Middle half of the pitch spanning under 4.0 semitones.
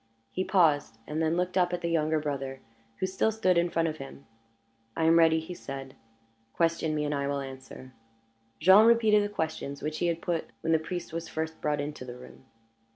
Yes: average, 3.4 semitones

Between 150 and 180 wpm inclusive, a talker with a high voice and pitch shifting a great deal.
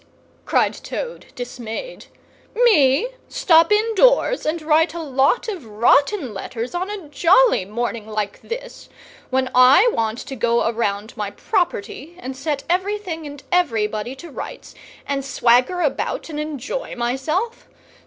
No: slow, 135 wpm; very high, 285 Hz; wide, 7.3 semitones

